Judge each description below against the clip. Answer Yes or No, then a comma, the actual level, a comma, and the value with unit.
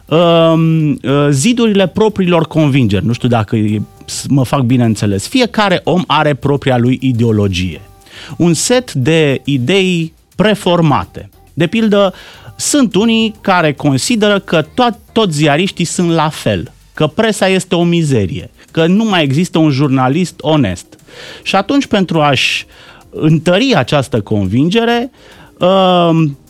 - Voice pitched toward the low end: No, medium, 160 Hz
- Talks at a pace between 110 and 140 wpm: Yes, average, 125 wpm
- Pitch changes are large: Yes, wide, 6.2 semitones